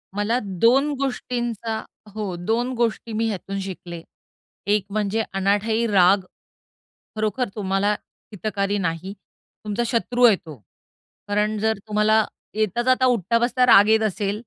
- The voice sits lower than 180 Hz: No, high, 215 Hz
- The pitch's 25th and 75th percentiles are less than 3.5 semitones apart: Yes, average, 2.8 semitones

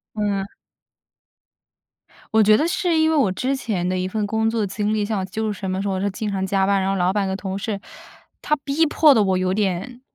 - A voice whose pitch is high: Yes, high, 205 Hz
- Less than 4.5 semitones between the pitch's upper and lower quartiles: Yes, average, 2.7 semitones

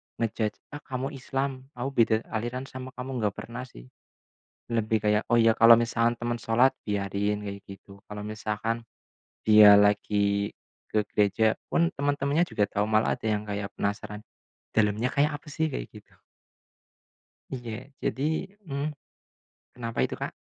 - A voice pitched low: Yes, low, 115 Hz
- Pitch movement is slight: No, average, 3.5 semitones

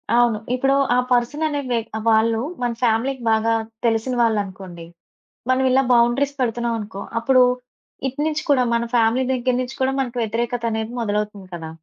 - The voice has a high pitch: Yes, high, 235 Hz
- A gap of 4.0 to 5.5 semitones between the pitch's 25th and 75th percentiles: No, narrow, 2.6 semitones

